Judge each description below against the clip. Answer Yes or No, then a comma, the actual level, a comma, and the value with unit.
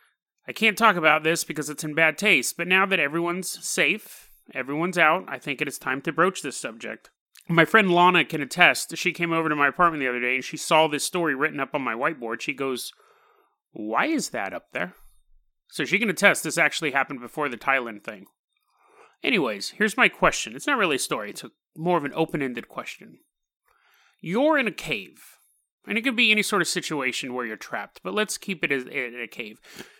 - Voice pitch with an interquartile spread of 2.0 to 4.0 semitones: No, average, 4.4 semitones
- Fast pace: Yes, fast, 210 wpm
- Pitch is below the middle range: No, medium, 160 Hz